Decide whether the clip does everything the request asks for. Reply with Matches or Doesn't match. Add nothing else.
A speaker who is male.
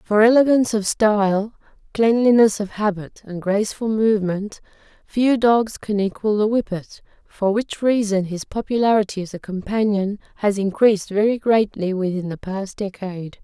Doesn't match